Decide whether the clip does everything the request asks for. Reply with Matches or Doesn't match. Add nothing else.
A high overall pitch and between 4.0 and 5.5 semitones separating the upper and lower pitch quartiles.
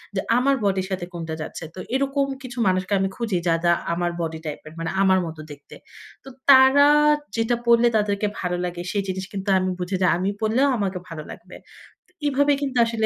Matches